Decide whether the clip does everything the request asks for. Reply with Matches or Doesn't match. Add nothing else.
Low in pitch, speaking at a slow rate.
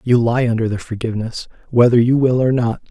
Doesn't match